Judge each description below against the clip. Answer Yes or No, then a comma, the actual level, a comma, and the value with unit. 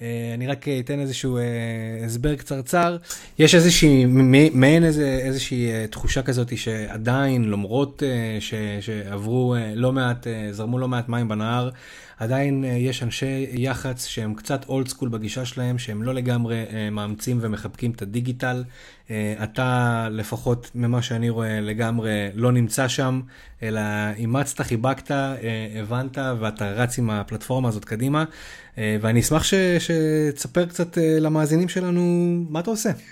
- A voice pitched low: Yes, low, 125 Hz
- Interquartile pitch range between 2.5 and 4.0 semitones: Yes, average, 3.4 semitones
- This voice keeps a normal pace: Yes, average, 140 wpm